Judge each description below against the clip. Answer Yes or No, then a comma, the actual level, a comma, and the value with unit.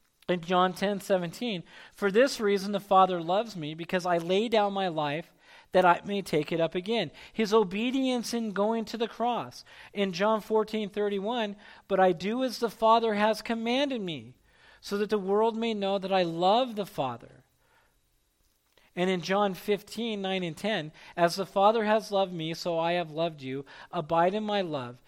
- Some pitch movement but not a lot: Yes, average, 3.8 semitones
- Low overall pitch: No, high, 195 Hz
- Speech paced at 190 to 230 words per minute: No, average, 175 wpm